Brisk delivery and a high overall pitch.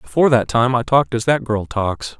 No: fast, 245 wpm; low, 120 Hz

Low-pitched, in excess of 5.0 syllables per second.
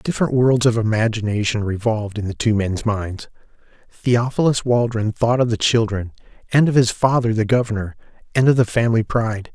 Yes: low, 115 Hz; 5.5 syllables/s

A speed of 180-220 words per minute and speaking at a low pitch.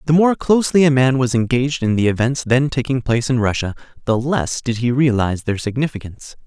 Yes: fast, 205 wpm; low, 130 Hz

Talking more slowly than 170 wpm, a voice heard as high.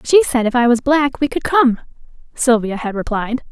No: fast, 205 wpm; very high, 250 Hz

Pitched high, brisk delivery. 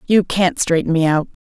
No: medium, 170 Hz; fast, 210 wpm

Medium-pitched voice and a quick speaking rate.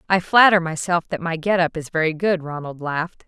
Yes: medium, 170 Hz; fast, 220 wpm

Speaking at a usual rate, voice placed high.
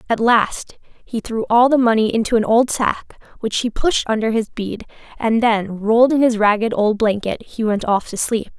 No: fast, 210 wpm; high, 225 Hz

